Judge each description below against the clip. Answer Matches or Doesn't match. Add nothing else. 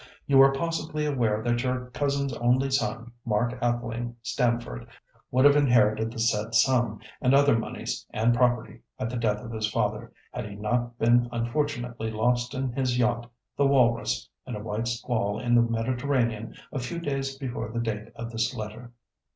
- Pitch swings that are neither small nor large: Doesn't match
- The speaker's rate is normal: Matches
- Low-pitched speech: Matches